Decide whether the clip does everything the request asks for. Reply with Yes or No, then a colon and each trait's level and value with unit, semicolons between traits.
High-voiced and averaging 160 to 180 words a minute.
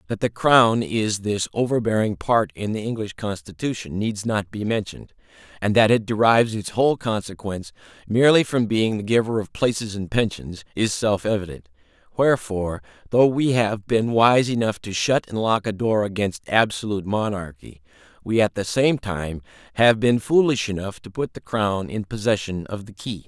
No: low, 105 Hz; average, 175 wpm